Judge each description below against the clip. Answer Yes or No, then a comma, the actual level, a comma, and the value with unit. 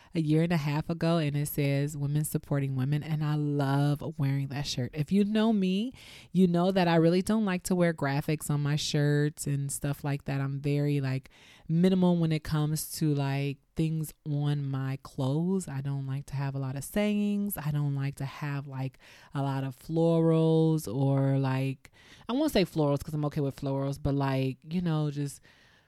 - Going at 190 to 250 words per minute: Yes, average, 200 wpm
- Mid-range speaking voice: Yes, medium, 145 Hz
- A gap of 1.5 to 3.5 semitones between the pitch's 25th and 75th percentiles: Yes, average, 2.9 semitones